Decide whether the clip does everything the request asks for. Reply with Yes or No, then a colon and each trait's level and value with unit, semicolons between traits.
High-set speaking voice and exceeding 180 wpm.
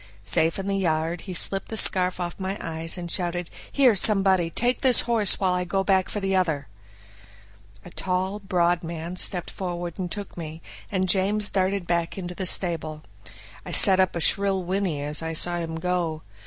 No: medium, 180 Hz; average, 190 wpm